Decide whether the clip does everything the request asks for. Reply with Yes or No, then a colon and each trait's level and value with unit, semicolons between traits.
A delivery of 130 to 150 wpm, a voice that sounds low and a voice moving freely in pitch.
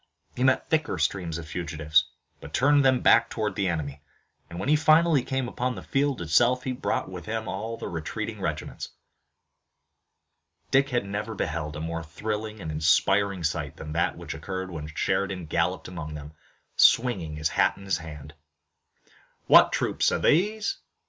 No: average, 165 wpm; very low, 95 Hz; wide, 7.9 semitones